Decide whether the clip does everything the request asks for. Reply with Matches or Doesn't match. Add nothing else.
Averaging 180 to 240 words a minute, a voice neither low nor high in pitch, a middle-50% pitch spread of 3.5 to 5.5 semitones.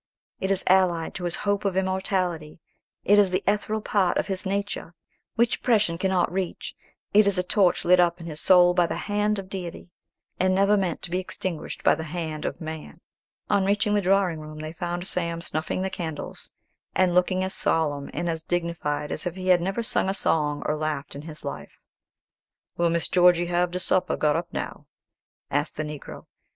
Doesn't match